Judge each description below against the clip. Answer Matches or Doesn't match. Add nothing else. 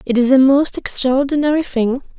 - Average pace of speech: Matches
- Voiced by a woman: Matches